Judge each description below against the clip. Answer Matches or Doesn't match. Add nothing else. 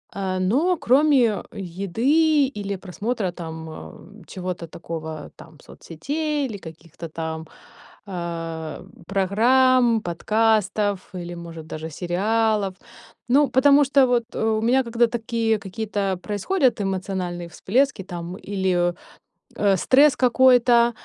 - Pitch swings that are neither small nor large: Doesn't match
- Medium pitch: Doesn't match